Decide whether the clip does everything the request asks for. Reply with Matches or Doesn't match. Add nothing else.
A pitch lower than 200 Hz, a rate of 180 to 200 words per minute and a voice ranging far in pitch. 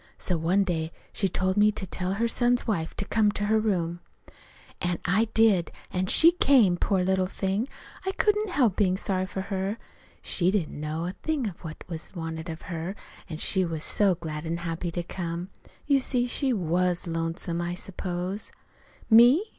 Doesn't match